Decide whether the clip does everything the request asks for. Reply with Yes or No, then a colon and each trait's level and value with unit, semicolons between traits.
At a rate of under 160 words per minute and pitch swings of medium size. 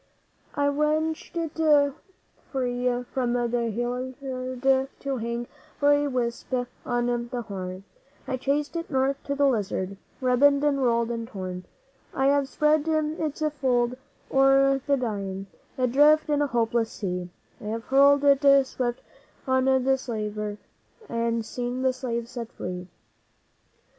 Yes: average, 140 wpm; average, 3.1 semitones